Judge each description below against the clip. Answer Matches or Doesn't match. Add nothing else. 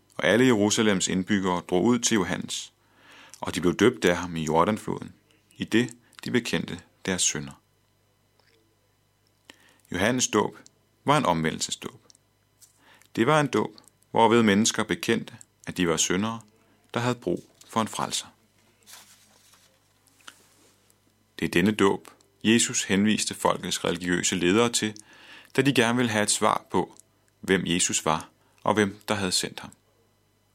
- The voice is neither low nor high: Doesn't match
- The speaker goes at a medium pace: Doesn't match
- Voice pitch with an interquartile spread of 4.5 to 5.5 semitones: Doesn't match